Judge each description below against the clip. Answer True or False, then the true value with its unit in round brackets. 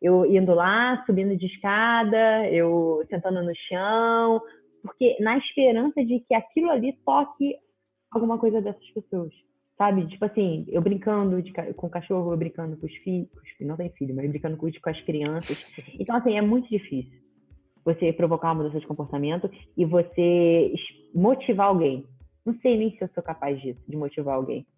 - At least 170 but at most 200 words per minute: True (180 wpm)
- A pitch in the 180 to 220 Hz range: True (185 Hz)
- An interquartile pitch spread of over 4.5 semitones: True (5.4 semitones)